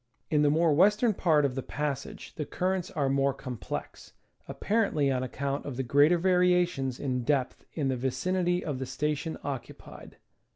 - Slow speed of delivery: No, average, 165 wpm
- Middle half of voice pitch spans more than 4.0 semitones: Yes, average, 4.8 semitones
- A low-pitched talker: No, medium, 145 Hz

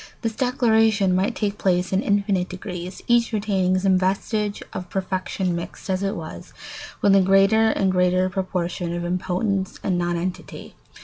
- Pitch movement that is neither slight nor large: No, narrow, 1.9 semitones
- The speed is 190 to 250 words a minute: No, average, 150 wpm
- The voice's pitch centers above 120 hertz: Yes, high, 190 Hz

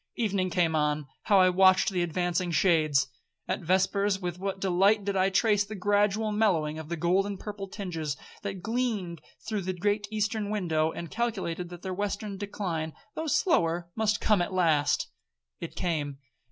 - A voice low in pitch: No, medium, 185 Hz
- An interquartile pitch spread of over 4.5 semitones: No, average, 3.3 semitones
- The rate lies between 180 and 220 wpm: No, average, 165 wpm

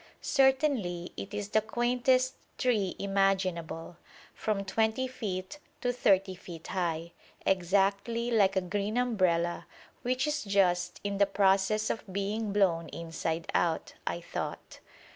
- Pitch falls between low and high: No, high, 200 Hz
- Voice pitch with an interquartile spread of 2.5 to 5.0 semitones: Yes, average, 3.8 semitones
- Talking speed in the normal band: No, slow, 125 wpm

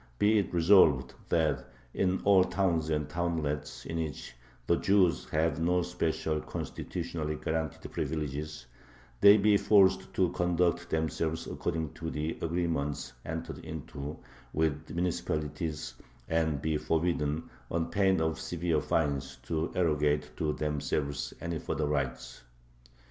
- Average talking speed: No, slow, 125 wpm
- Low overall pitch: Yes, very low, 80 Hz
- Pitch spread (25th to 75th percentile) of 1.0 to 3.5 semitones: Yes, narrow, 2.5 semitones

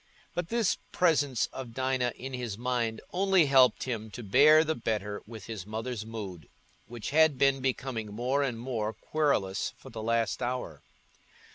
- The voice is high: No, low, 125 Hz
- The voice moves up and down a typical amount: Yes, average, 3.7 semitones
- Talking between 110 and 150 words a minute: No, average, 160 wpm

